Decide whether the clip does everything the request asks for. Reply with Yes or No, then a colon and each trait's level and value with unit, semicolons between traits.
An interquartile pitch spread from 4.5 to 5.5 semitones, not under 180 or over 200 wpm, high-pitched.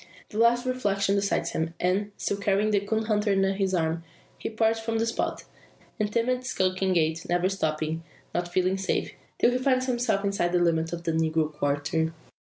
Yes: average, 4.8 semitones; average, 190 wpm; high, 195 Hz